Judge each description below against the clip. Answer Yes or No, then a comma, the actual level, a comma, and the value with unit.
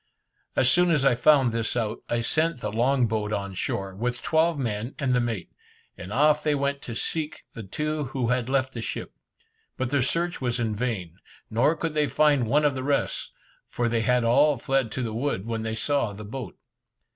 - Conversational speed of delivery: No, fast, 210 wpm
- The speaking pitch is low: Yes, low, 125 Hz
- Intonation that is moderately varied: Yes, average, 4.2 semitones